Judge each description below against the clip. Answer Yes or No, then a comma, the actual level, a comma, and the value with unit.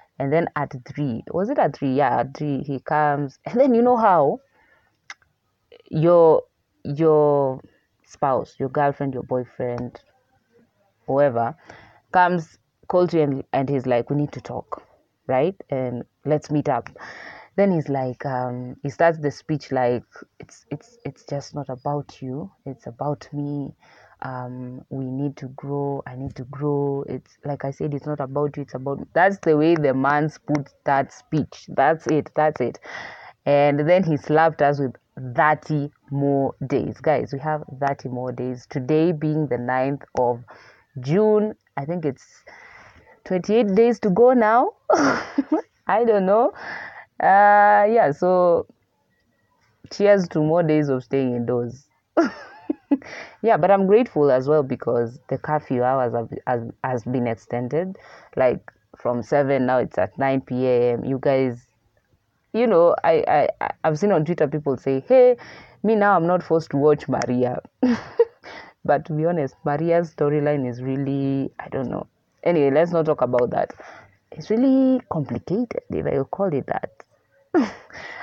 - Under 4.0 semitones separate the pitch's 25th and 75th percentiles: No, average, 4.5 semitones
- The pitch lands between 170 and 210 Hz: No, medium, 145 Hz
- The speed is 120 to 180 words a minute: Yes, average, 155 wpm